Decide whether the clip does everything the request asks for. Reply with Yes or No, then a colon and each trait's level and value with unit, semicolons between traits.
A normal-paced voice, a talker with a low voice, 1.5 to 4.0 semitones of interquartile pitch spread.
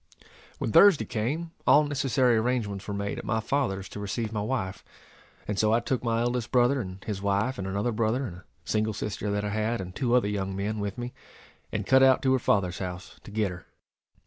No: fast, 220 wpm; low, 110 Hz; average, 3.7 semitones